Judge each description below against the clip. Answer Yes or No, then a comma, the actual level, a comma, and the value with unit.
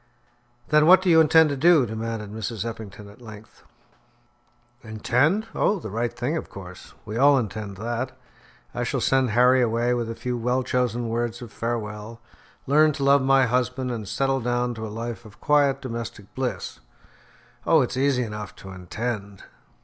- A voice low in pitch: Yes, low, 120 Hz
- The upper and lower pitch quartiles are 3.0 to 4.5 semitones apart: Yes, average, 3.3 semitones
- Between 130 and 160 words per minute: No, average, 170 wpm